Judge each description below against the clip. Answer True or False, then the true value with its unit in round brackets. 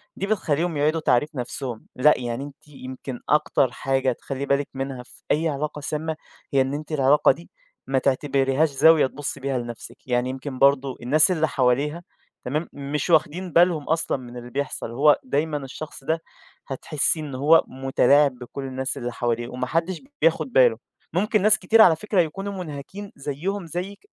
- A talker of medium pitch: True (145 Hz)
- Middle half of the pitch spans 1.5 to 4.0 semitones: True (3.5 semitones)